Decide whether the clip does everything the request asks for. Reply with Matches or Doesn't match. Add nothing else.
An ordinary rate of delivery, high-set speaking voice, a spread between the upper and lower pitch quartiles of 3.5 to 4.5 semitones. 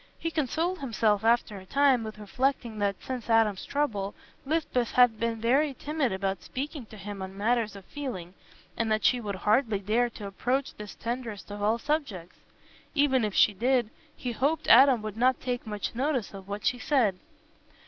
Matches